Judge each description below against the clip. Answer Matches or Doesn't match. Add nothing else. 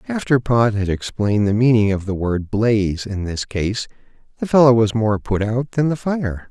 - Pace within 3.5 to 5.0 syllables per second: Matches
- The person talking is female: Doesn't match